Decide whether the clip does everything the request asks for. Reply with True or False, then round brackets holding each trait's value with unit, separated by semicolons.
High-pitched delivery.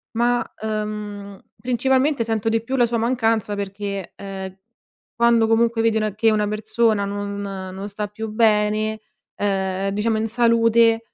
True (215 Hz)